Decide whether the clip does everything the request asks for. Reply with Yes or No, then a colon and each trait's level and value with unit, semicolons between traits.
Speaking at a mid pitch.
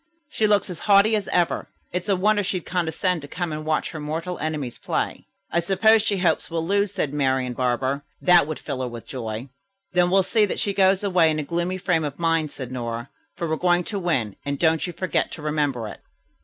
Yes: medium, 165 Hz